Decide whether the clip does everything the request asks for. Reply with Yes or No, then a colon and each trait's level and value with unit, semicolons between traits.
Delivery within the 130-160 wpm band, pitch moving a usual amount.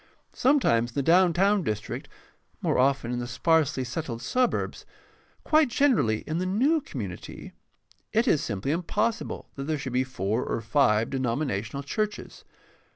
No: average, 150 wpm; wide, 8.6 semitones